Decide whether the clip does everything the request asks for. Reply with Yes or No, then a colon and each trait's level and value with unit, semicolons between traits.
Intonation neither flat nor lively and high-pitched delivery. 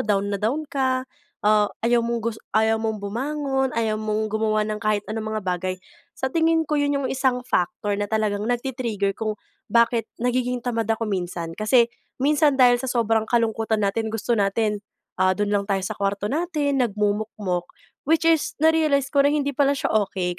Yes: average, 4.0 semitones; high, 225 Hz